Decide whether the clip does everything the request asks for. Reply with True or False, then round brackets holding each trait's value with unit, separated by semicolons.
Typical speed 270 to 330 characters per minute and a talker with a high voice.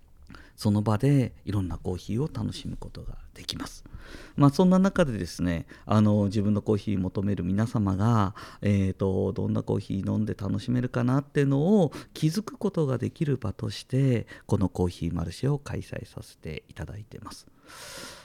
False (295 characters per minute; 105 Hz)